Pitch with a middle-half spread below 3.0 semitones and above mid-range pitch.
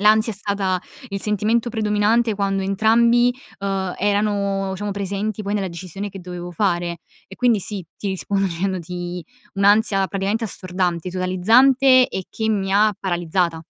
Yes: narrow, 2.5 semitones; high, 195 Hz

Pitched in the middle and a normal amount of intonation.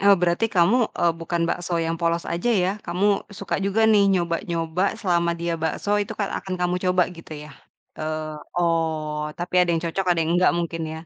No: medium, 170 Hz; narrow, 1.7 semitones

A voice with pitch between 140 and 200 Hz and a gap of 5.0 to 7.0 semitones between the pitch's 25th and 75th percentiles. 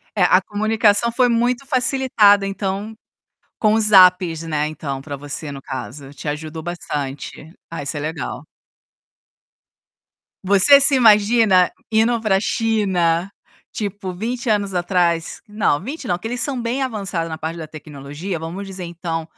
Yes: high, 190 Hz; average, 5.3 semitones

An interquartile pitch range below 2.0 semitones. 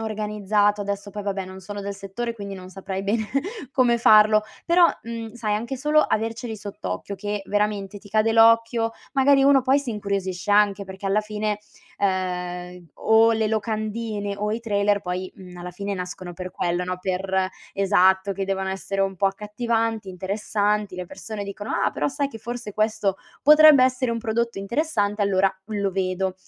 No: average, 2.7 semitones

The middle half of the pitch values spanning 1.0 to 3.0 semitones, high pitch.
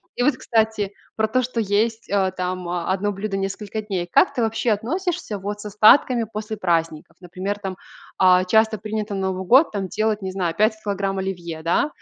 Yes: average, 2.7 semitones; high, 205 Hz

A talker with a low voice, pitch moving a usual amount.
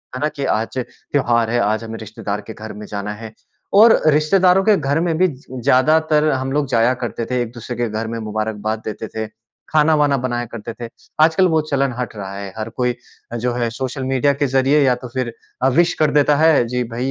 Yes: low, 125 Hz; average, 4.5 semitones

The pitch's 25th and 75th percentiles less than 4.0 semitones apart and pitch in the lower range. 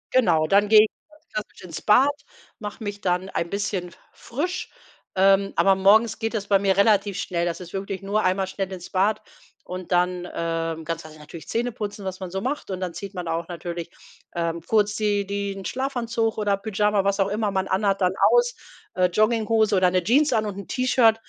No: average, 2.9 semitones; high, 195 Hz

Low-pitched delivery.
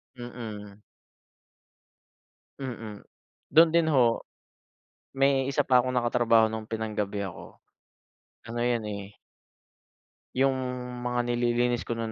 Yes: low, 120 Hz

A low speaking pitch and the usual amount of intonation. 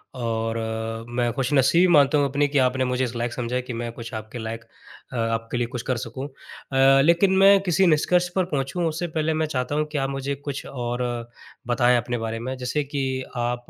Yes: low, 130 Hz; average, 3.6 semitones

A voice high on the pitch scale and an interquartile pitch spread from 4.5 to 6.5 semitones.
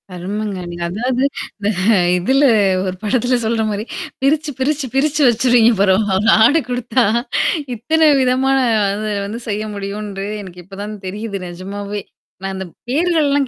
Yes: high, 220 Hz; average, 4.8 semitones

